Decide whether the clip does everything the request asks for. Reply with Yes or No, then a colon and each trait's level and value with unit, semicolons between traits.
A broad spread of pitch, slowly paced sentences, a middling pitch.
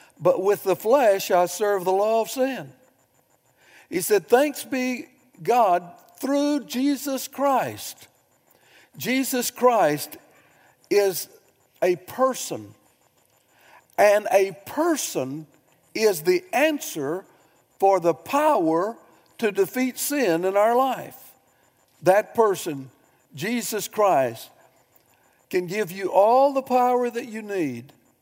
No: wide, 6.3 semitones; slow, 110 wpm; high, 220 Hz